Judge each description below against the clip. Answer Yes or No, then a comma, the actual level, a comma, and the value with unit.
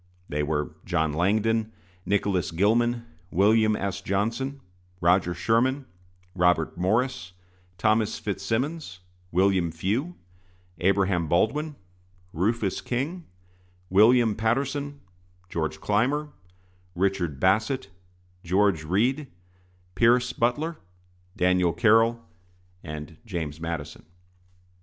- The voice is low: Yes, low, 100 Hz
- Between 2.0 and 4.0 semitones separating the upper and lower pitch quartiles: No, average, 5.2 semitones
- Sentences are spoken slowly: Yes, slow, 85 wpm